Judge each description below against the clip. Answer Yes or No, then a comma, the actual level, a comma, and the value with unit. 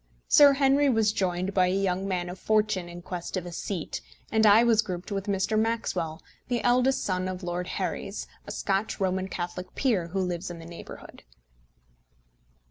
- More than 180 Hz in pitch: Yes, high, 190 Hz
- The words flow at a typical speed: Yes, average, 180 wpm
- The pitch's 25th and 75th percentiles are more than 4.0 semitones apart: No, average, 3.4 semitones